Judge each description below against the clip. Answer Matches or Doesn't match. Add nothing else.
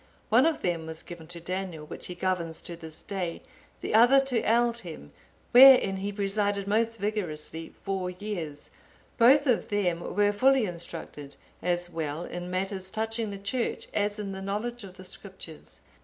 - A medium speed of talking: Matches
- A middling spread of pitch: Matches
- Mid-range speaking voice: Doesn't match